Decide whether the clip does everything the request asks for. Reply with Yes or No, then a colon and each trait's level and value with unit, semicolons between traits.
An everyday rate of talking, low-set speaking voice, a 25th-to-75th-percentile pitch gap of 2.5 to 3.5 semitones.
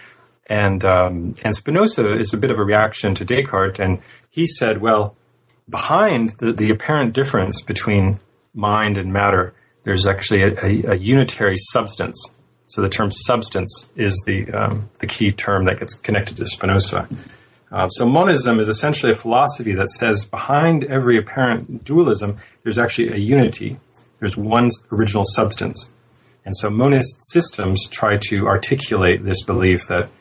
Yes: average, 155 wpm; low, 110 Hz; average, 3.2 semitones